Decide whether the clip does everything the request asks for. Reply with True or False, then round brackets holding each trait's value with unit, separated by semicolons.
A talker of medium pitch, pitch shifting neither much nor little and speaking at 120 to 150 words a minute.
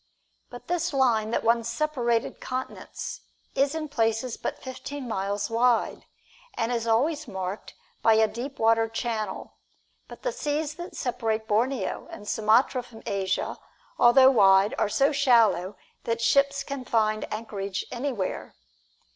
False (235 Hz; 3.9 semitones; 140 wpm)